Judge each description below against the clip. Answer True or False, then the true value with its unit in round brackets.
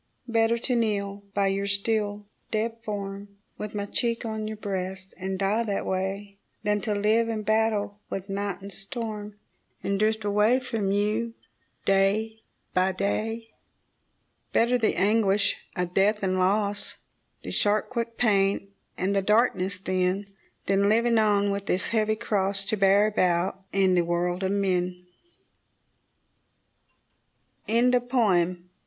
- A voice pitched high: True (205 Hz)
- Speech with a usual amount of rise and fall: False (2.1 semitones)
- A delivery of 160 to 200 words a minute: False (140 wpm)